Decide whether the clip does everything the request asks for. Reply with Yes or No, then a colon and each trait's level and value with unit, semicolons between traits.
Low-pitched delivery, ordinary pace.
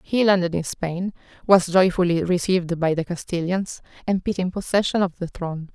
No: medium, 180 Hz; average, 175 wpm